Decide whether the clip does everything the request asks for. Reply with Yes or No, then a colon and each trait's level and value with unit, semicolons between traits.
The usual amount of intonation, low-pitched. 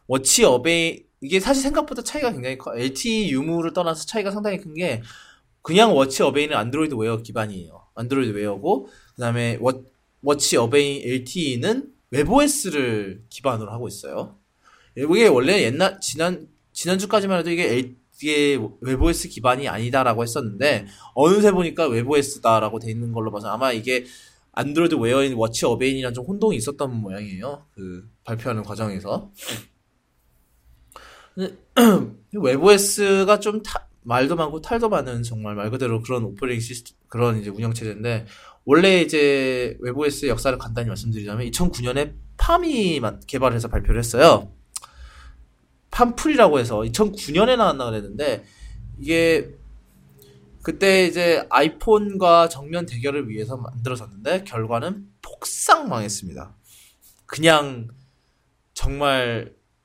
No: wide, 7.0 semitones; low, 130 Hz